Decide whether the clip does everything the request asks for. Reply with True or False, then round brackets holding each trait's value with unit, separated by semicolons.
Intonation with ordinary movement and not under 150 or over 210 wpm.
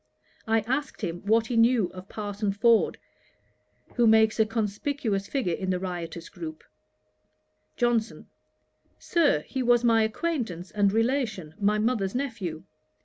False (3.6 semitones; 135 wpm)